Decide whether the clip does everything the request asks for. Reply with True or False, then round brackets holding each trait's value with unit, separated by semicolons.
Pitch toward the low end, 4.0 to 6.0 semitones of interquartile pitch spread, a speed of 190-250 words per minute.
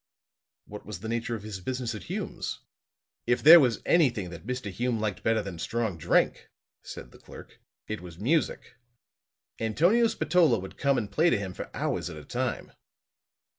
False (115 Hz; 4.3 semitones; 175 wpm)